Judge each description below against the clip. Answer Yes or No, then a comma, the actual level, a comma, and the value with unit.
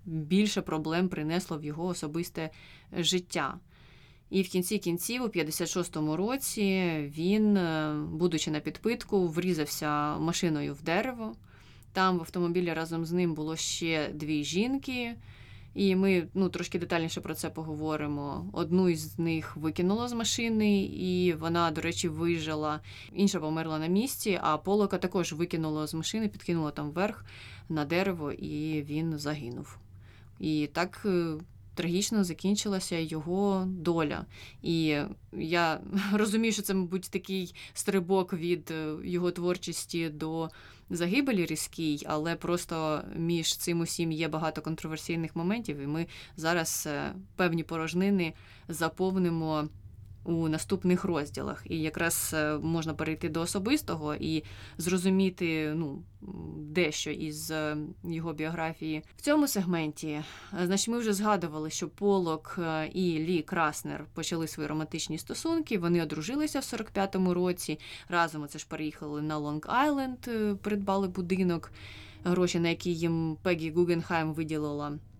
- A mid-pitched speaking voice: Yes, medium, 165 Hz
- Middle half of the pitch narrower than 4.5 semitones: Yes, average, 3.1 semitones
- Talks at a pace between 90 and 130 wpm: Yes, average, 125 wpm